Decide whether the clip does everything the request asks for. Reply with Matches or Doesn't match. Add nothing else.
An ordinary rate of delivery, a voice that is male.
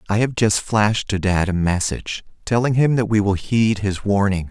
Doesn't match